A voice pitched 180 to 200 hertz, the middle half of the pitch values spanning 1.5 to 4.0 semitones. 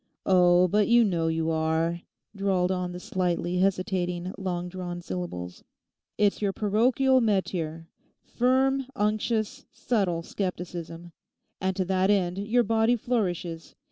Yes: medium, 185 Hz; average, 3.3 semitones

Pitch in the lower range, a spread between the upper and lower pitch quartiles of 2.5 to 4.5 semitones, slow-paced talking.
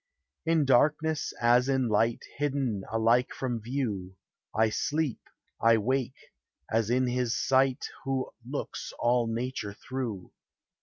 Yes: low, 125 Hz; average, 2.9 semitones; slow, 120 wpm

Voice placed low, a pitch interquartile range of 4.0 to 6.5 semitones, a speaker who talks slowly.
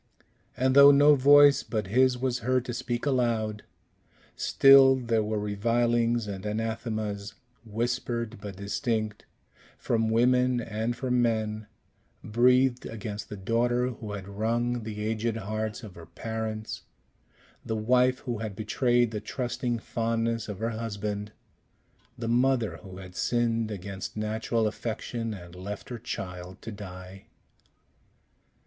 No: low, 115 Hz; narrow, 2.5 semitones; slow, 130 wpm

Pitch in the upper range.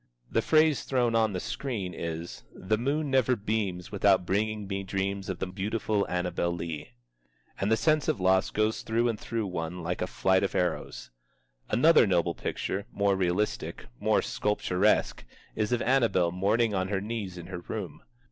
No: low, 100 Hz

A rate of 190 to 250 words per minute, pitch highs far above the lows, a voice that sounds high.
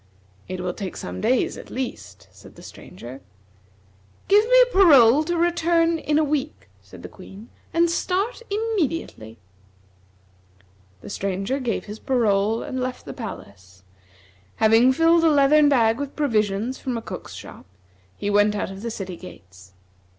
No: average, 155 wpm; wide, 8.2 semitones; high, 240 Hz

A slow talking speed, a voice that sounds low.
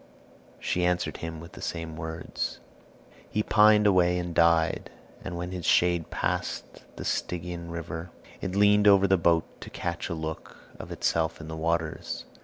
No: average, 165 wpm; very low, 85 Hz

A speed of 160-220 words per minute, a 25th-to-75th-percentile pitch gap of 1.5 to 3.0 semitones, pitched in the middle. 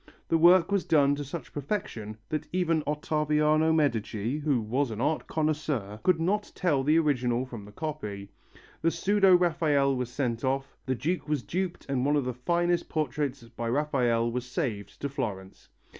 No: average, 175 wpm; average, 4.5 semitones; medium, 145 Hz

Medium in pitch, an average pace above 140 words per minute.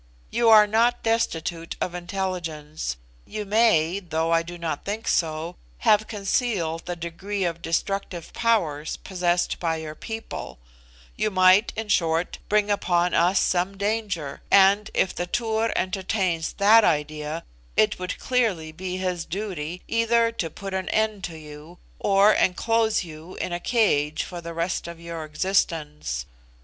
Yes: medium, 180 Hz; average, 150 wpm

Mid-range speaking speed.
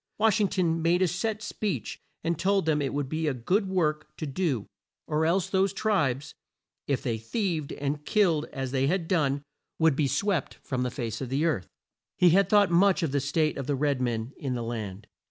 No: fast, 210 wpm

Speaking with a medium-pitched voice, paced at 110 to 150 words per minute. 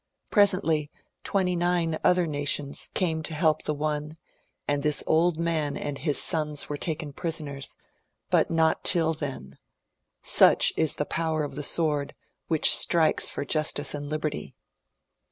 Yes: medium, 155 Hz; average, 145 wpm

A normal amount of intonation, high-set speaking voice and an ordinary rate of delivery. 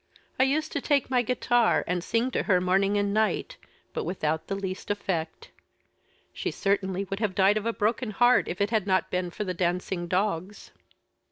Yes: average, 3.8 semitones; high, 200 Hz; average, 190 wpm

